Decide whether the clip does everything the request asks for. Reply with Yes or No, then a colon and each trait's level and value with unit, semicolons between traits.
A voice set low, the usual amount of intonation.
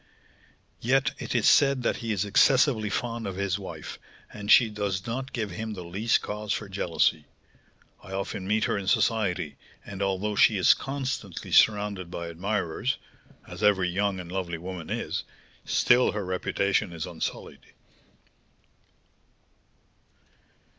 Yes: low, 100 Hz; average, 3.1 semitones